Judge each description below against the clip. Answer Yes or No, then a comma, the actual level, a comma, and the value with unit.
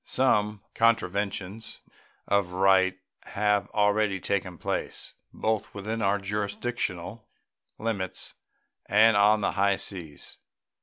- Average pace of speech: No, slow, 100 wpm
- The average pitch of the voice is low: Yes, low, 100 Hz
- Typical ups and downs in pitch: No, narrow, 1.9 semitones